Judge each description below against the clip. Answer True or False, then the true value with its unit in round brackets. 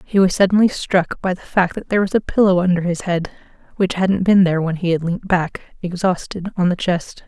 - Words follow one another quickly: True (230 wpm)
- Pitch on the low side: False (180 Hz)